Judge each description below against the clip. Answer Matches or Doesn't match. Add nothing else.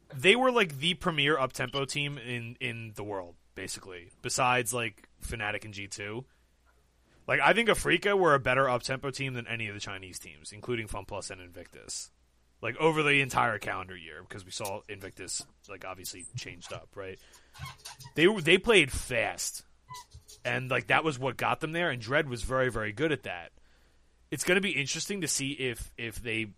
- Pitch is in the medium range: Doesn't match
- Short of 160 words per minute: Doesn't match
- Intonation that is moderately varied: Doesn't match